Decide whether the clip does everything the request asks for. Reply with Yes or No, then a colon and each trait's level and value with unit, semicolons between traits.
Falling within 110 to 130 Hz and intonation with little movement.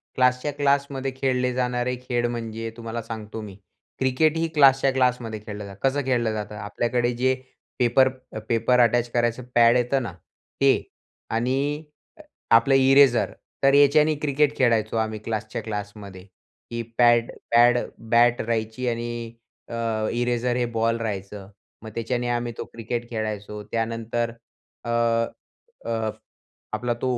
Yes: low, 120 Hz; narrow, 2.2 semitones